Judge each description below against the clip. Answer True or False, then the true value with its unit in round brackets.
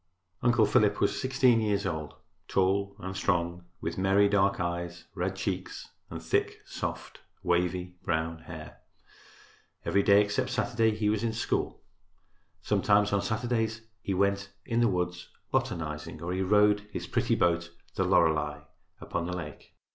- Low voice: True (100 Hz)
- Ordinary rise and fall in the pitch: True (3.1 semitones)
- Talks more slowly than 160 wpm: True (145 wpm)